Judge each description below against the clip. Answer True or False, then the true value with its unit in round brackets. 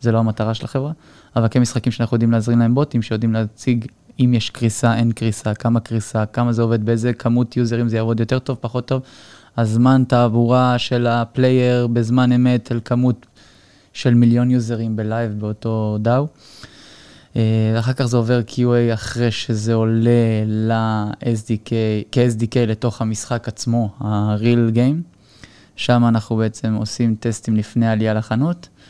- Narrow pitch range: True (1.6 semitones)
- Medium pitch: False (115 Hz)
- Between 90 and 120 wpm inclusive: False (145 wpm)